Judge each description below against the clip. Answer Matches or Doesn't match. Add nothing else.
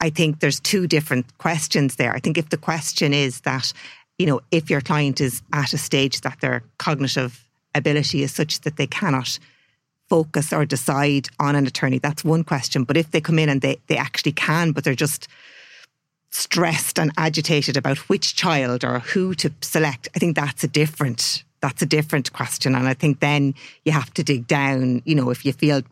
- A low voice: Doesn't match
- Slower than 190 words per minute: Doesn't match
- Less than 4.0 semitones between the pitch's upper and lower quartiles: Matches